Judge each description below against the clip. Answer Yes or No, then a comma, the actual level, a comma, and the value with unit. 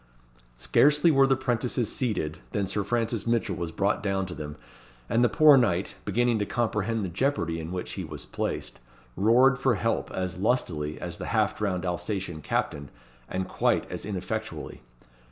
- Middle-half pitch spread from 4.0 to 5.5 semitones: Yes, average, 5.1 semitones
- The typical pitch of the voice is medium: No, low, 105 Hz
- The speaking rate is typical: Yes, average, 170 wpm